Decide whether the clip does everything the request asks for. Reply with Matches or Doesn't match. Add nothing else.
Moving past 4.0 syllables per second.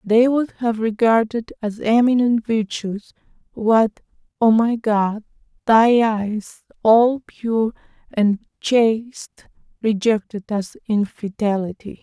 Doesn't match